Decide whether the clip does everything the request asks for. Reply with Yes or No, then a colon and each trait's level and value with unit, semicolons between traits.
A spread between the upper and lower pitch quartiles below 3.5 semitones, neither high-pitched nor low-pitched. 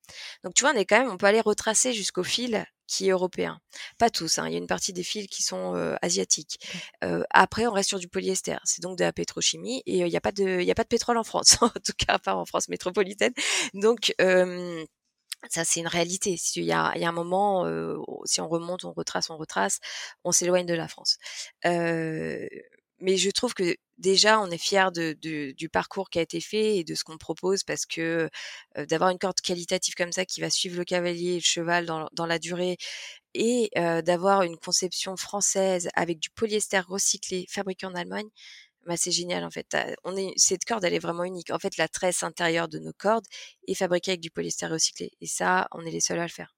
Yes: average, 3.0 semitones; medium, 180 Hz